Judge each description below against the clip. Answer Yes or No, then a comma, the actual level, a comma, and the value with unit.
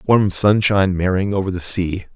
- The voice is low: Yes, very low, 95 Hz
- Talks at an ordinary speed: Yes, average, 165 wpm